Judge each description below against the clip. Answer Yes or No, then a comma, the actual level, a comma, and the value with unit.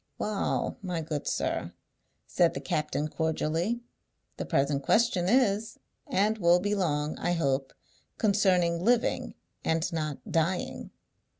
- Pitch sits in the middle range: Yes, medium, 175 Hz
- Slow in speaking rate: Yes, slow, 120 wpm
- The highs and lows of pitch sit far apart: No, average, 4.8 semitones